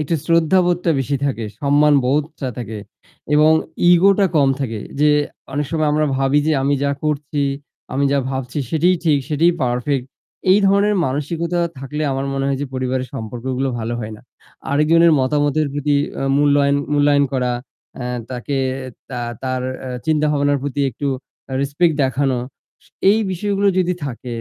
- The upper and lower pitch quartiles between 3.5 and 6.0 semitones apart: No, average, 2.8 semitones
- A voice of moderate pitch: Yes, medium, 145 Hz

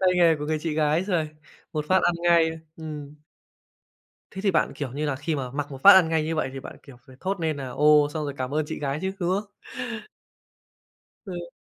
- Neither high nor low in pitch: Yes, medium, 155 Hz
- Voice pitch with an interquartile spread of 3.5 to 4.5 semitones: No, average, 3.0 semitones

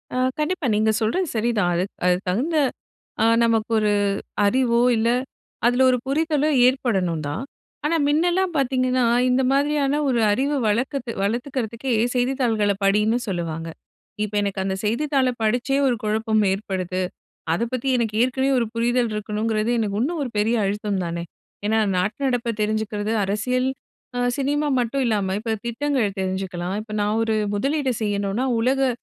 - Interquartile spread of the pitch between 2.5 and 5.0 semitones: Yes, average, 4.2 semitones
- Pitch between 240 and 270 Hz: No, high, 230 Hz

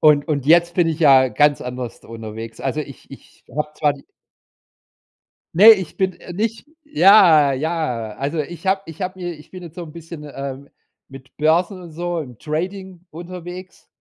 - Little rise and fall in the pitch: No, average, 4.3 semitones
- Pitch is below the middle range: No, medium, 160 Hz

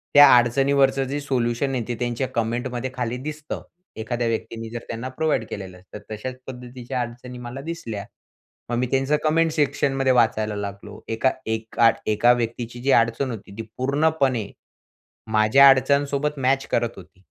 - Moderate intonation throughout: Yes, average, 3.1 semitones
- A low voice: Yes, low, 125 Hz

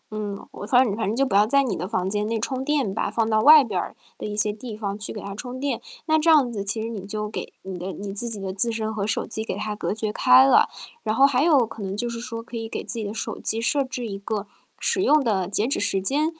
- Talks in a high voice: Yes, high, 220 Hz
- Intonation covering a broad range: No, average, 3.5 semitones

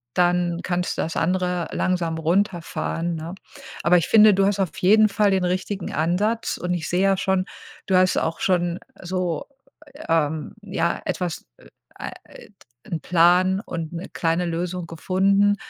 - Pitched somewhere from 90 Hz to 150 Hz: No, medium, 180 Hz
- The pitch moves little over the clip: Yes, narrow, 2.1 semitones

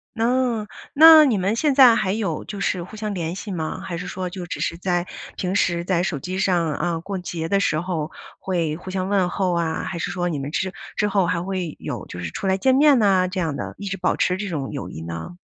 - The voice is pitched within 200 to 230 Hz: No, medium, 185 Hz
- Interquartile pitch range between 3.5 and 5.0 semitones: No, average, 2.9 semitones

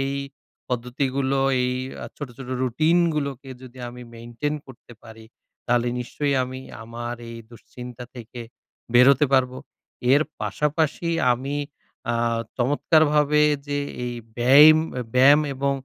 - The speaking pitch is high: No, low, 130 Hz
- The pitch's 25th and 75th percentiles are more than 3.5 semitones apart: No, average, 2.9 semitones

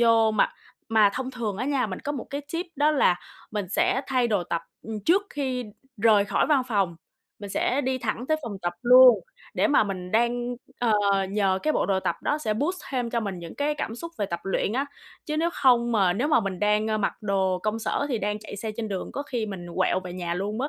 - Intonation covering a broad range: No, average, 4.7 semitones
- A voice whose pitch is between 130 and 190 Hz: No, high, 225 Hz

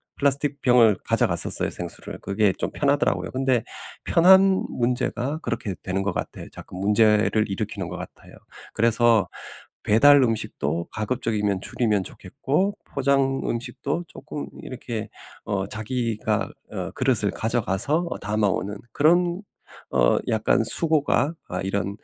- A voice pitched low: Yes, low, 115 Hz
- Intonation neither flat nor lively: Yes, average, 5.0 semitones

